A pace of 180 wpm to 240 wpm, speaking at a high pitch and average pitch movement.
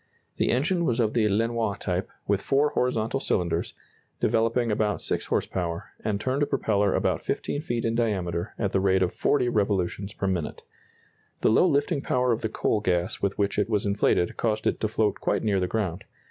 No: average, 200 wpm; low, 105 Hz; average, 3.4 semitones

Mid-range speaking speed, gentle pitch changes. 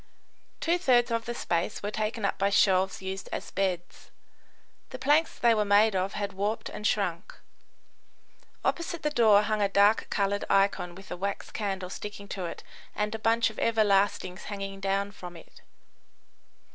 Yes: average, 170 wpm; narrow, 2.2 semitones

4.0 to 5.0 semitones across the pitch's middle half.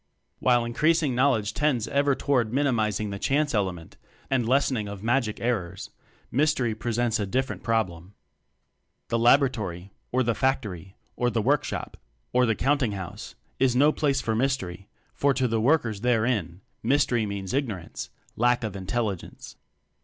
Yes: average, 4.4 semitones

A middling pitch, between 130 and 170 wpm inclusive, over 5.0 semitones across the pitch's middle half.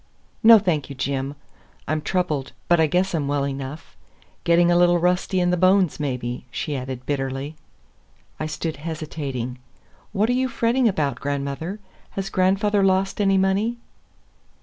Yes: medium, 165 Hz; average, 150 wpm; wide, 5.5 semitones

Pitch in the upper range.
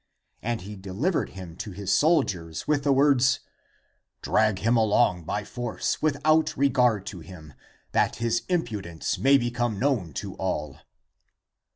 No: low, 110 Hz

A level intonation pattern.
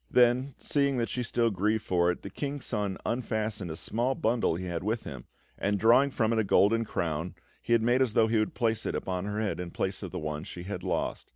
No: average, 4.4 semitones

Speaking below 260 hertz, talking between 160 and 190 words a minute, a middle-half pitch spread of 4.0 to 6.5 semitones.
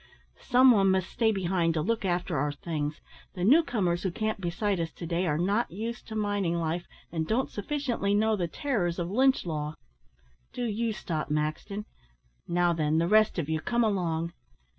Yes: medium, 185 Hz; average, 185 wpm; average, 4.6 semitones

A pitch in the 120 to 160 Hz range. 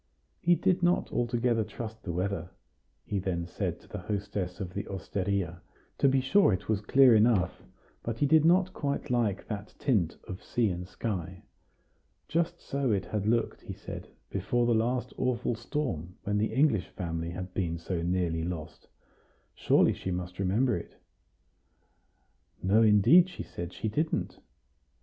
No: low, 105 Hz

